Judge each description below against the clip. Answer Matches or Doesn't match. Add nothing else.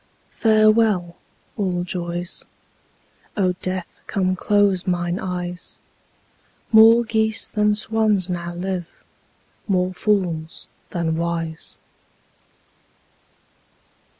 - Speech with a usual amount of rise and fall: Matches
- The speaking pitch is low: Doesn't match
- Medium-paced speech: Doesn't match